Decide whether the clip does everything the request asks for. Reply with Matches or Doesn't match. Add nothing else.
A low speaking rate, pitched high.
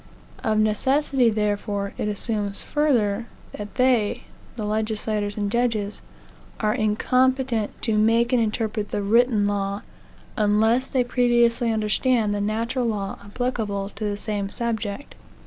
Matches